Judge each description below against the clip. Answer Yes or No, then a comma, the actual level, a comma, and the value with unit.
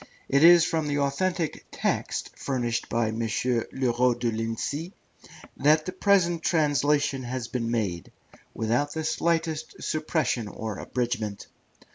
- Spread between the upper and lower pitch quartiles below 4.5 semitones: No, average, 5.3 semitones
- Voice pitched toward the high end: No, low, 135 Hz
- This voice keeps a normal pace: No, slow, 130 wpm